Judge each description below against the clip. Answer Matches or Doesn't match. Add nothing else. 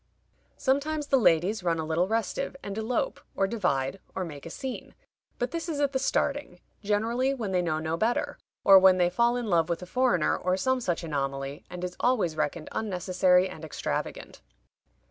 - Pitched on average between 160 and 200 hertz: Matches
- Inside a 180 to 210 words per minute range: Matches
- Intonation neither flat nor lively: Doesn't match